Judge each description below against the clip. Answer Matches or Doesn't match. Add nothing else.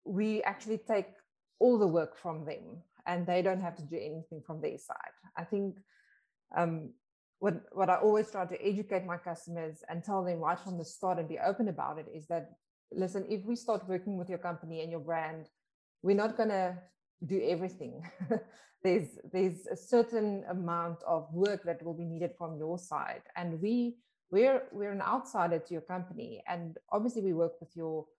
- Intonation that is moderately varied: Matches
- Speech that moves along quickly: Doesn't match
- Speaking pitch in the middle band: Matches